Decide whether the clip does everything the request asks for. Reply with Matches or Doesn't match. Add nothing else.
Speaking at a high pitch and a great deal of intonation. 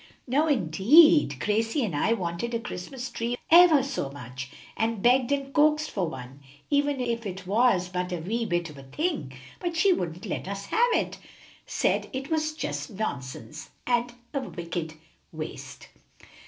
Matches